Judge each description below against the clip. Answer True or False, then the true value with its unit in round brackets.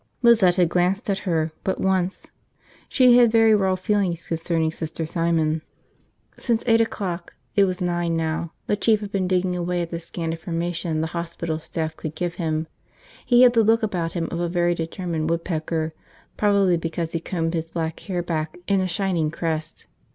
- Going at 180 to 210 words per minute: True (190 wpm)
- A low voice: False (175 Hz)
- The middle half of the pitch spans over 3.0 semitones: False (2.7 semitones)